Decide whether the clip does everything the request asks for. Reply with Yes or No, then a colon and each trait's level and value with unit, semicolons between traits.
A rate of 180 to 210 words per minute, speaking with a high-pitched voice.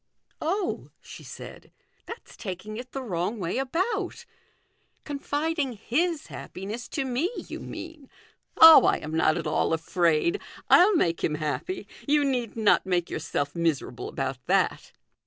No: average, 155 wpm; high, 245 Hz